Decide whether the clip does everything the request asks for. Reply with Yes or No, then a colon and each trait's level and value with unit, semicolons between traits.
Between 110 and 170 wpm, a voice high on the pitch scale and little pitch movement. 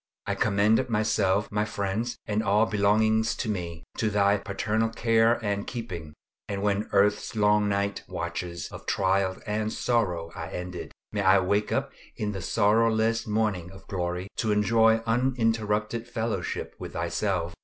No: average, 150 wpm; low, 105 Hz; narrow, 2.3 semitones